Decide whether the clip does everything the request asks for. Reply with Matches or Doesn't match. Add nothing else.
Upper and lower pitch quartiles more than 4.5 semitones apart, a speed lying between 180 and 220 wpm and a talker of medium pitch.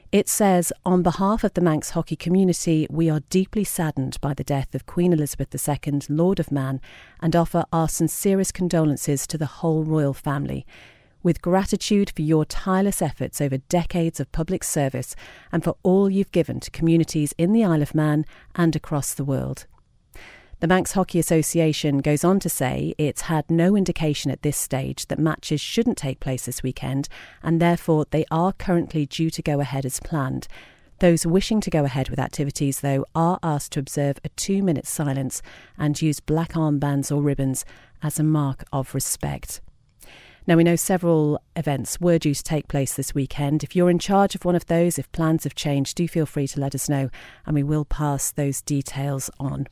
Doesn't match